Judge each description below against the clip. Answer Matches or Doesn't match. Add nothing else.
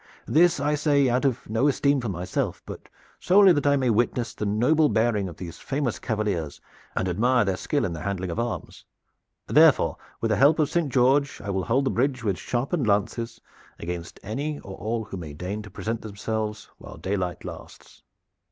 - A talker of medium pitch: Doesn't match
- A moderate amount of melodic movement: Doesn't match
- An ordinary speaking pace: Matches